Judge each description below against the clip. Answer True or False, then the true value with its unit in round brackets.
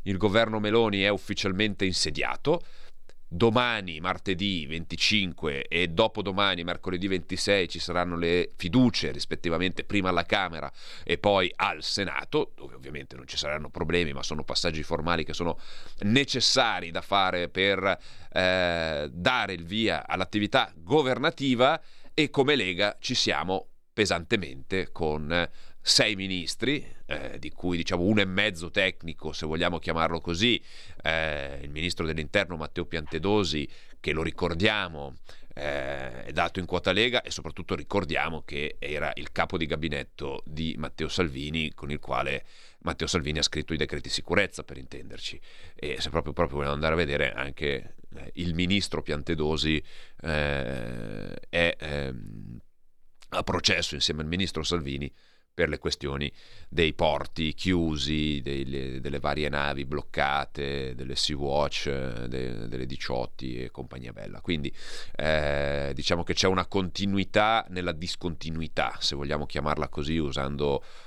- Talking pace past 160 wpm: False (135 wpm)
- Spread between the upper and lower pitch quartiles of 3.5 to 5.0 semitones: True (4.2 semitones)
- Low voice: True (85 Hz)